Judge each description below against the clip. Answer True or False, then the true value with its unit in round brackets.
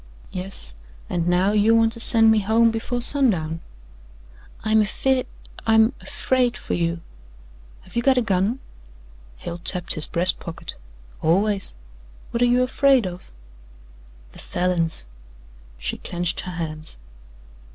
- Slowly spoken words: True (130 wpm)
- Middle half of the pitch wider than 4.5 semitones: True (5.1 semitones)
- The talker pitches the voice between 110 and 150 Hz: False (205 Hz)